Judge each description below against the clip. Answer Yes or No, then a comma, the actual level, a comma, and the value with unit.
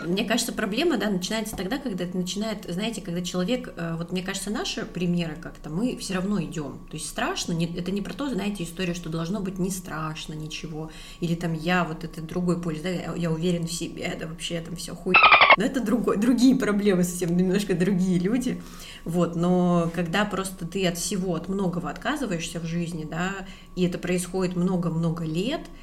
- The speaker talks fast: Yes, fast, 195 wpm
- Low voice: No, medium, 180 Hz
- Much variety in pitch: No, average, 2.8 semitones